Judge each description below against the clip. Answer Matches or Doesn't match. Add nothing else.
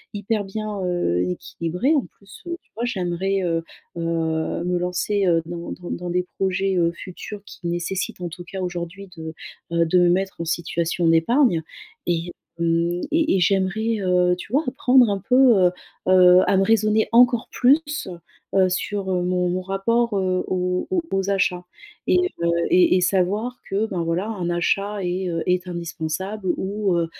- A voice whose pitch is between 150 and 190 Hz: Matches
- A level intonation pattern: Doesn't match